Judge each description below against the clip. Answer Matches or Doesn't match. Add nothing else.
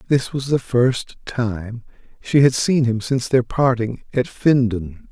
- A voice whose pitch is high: Doesn't match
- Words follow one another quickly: Doesn't match